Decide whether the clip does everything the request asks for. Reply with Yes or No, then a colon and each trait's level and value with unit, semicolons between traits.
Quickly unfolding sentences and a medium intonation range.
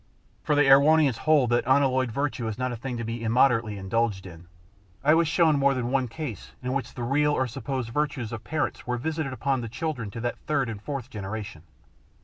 Yes: fast, 210 wpm; average, 3.7 semitones